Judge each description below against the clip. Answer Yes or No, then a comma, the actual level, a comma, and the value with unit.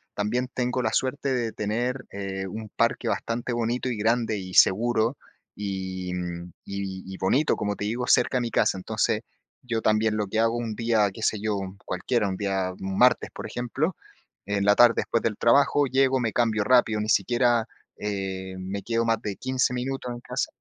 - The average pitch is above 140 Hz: No, low, 110 Hz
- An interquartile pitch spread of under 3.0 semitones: No, average, 3.3 semitones